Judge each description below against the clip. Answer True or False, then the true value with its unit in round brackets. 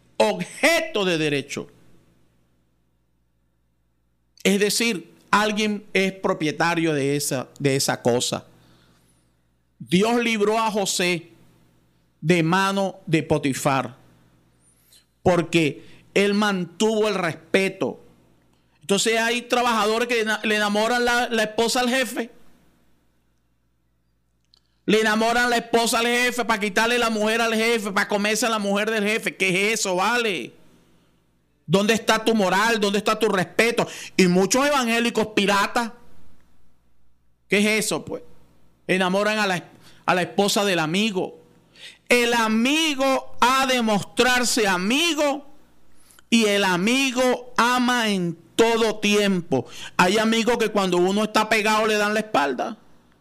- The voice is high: True (200 Hz)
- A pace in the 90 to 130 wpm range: True (125 wpm)